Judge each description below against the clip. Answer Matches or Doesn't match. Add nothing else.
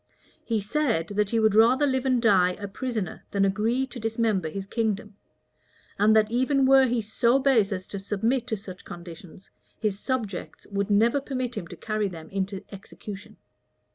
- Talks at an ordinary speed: Matches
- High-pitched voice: Matches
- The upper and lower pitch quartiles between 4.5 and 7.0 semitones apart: Doesn't match